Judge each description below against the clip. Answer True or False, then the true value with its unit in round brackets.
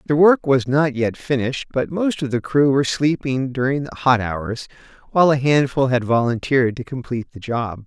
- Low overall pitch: True (130 Hz)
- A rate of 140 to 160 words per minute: False (200 wpm)